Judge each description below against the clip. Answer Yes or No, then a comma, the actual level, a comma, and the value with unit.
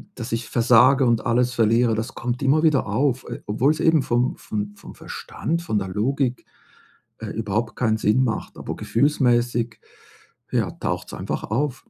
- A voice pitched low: Yes, low, 120 Hz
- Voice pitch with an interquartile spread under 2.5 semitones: No, average, 2.9 semitones